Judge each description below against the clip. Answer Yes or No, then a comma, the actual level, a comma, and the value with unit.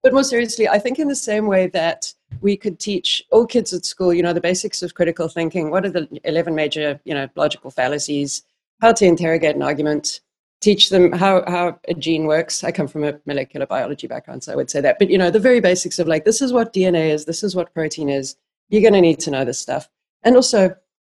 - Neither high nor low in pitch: Yes, medium, 175 Hz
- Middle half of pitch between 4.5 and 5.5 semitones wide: Yes, average, 4.8 semitones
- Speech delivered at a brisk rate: Yes, fast, 240 wpm